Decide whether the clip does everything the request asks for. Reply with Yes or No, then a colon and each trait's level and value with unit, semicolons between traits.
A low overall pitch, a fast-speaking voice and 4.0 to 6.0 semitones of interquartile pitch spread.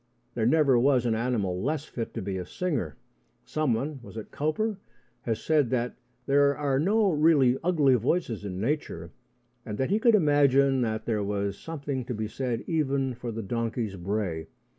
No: low, 130 Hz; average, 175 wpm; average, 5.1 semitones